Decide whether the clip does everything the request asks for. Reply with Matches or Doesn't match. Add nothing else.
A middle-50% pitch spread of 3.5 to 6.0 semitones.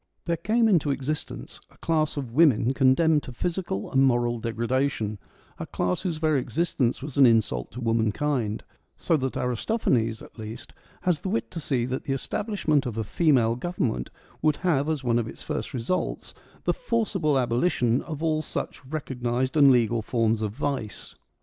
Matches